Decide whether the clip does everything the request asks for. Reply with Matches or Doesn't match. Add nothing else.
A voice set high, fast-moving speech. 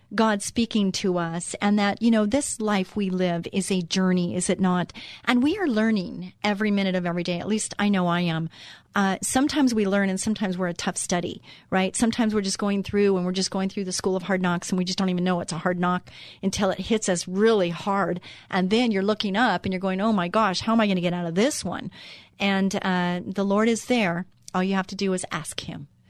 Matches